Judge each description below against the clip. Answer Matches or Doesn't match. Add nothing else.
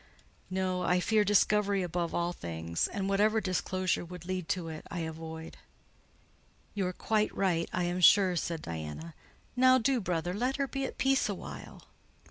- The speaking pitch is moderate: Matches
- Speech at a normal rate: Matches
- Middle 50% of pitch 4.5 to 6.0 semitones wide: Doesn't match